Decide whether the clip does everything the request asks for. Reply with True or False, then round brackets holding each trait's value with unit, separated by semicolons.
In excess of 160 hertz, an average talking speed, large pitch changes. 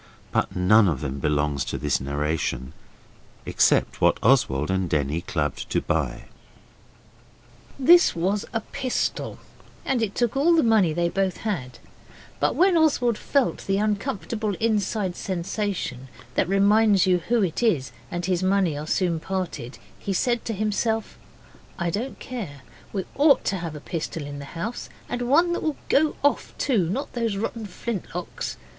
True (190 Hz; 160 wpm; 8.1 semitones)